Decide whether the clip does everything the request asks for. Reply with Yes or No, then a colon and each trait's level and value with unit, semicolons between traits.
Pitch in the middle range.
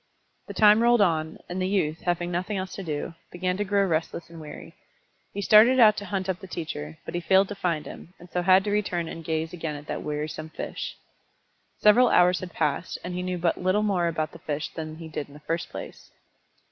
Yes: medium, 175 Hz